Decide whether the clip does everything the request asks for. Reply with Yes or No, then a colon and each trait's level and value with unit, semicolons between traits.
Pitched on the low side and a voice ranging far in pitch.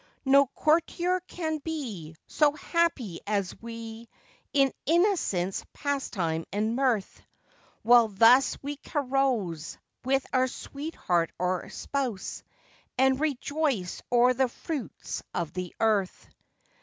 No: very high, 250 Hz; wide, 6.1 semitones